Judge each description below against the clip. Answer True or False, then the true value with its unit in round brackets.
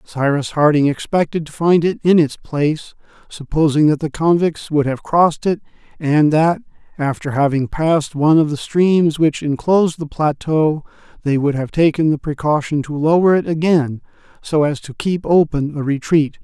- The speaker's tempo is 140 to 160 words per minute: False (170 wpm)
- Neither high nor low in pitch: True (155 Hz)